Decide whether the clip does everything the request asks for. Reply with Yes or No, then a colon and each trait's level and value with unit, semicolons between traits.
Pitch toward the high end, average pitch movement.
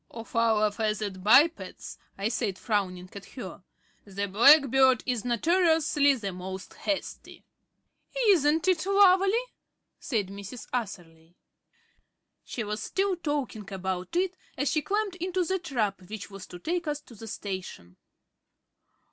No: high, 235 Hz; wide, 8.4 semitones